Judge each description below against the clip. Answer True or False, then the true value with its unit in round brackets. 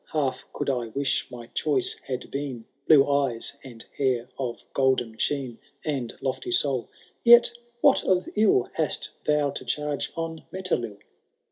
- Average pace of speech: True (150 wpm)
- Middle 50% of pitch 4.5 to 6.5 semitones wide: False (3.4 semitones)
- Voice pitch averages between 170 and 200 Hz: False (135 Hz)